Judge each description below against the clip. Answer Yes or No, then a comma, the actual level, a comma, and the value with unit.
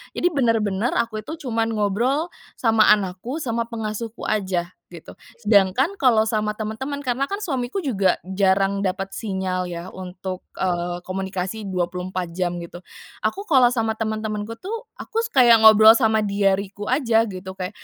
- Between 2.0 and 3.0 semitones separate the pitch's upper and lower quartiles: No, average, 3.8 semitones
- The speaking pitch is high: Yes, high, 215 Hz